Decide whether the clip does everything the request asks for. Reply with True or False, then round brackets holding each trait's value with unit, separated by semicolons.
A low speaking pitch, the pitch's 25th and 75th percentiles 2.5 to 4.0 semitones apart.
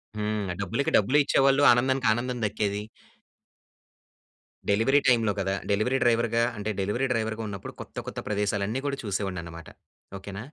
True (110 Hz; 3.5 semitones)